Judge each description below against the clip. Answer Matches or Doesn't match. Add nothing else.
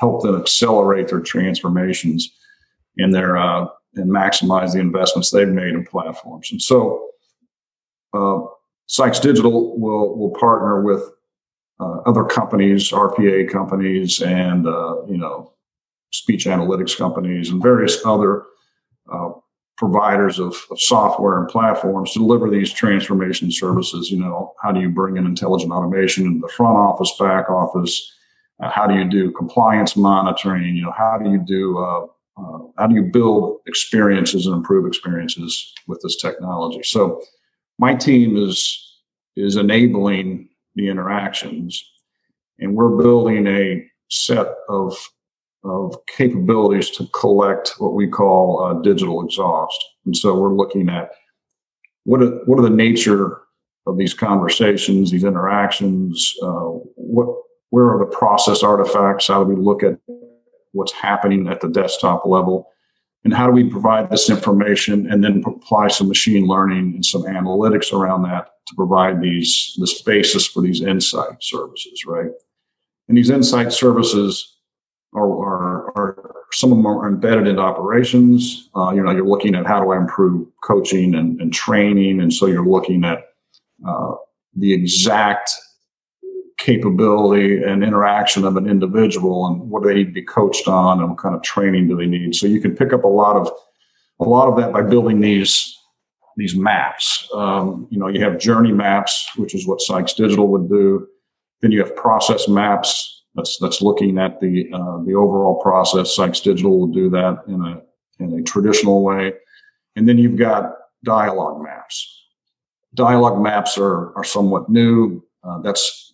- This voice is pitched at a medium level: Doesn't match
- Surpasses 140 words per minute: Matches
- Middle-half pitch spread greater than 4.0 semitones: Doesn't match